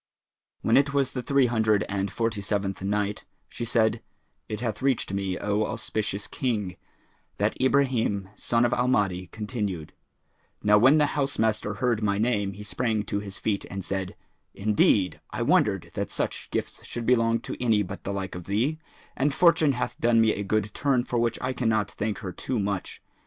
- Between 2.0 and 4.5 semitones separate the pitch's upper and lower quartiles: Yes, average, 3.5 semitones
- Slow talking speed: No, average, 185 wpm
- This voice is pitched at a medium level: No, low, 110 Hz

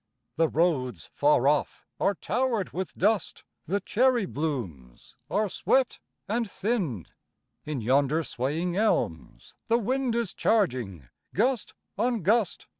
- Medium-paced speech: No, slow, 120 wpm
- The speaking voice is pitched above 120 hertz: Yes, medium, 185 Hz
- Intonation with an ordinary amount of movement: No, wide, 8.3 semitones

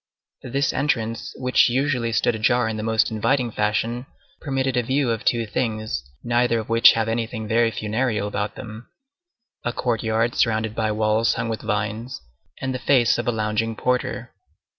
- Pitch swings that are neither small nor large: No, narrow, 2.3 semitones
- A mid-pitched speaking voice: No, low, 115 Hz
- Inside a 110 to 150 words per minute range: No, average, 160 wpm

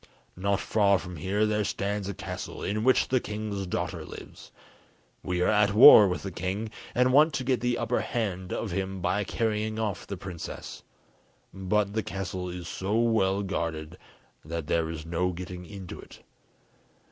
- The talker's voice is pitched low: Yes, low, 100 Hz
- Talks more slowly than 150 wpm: No, average, 170 wpm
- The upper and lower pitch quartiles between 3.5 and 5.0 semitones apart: No, average, 2.8 semitones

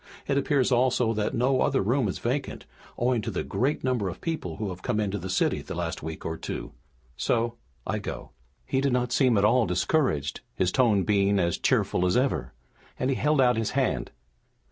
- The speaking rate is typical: No, fast, 210 wpm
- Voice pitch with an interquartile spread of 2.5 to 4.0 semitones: No, average, 4.8 semitones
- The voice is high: No, low, 120 Hz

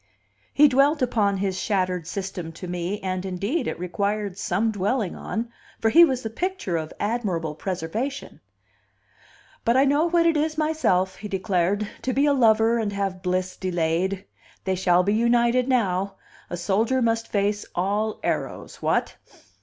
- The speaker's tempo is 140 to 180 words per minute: Yes, average, 160 wpm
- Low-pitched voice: No, high, 205 Hz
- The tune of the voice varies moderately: Yes, average, 4.6 semitones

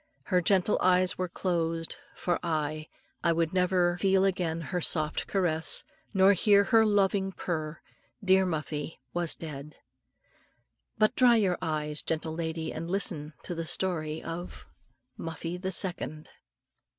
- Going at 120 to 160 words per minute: Yes, average, 140 wpm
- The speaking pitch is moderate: Yes, medium, 175 Hz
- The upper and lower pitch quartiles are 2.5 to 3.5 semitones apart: Yes, average, 3.0 semitones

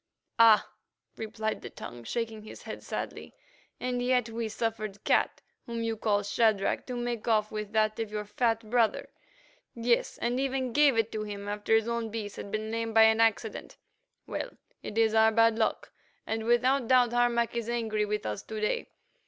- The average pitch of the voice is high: Yes, high, 225 Hz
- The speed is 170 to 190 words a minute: Yes, average, 180 wpm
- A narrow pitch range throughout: Yes, narrow, 1.7 semitones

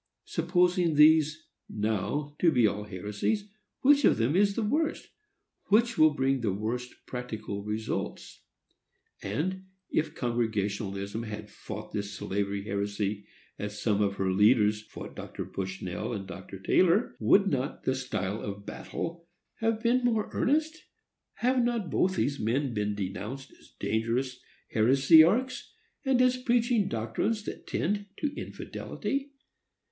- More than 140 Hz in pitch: No, low, 130 Hz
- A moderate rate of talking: No, slow, 130 wpm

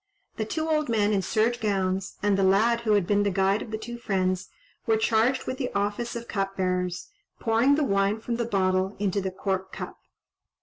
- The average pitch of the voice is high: Yes, high, 205 Hz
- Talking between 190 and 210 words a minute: Yes, fast, 205 wpm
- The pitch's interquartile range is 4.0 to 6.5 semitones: No, average, 3.3 semitones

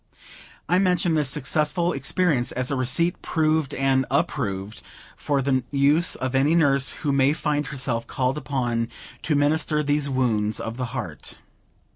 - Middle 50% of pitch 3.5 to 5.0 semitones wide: No, average, 3.0 semitones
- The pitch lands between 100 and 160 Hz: Yes, medium, 140 Hz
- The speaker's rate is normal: Yes, average, 155 wpm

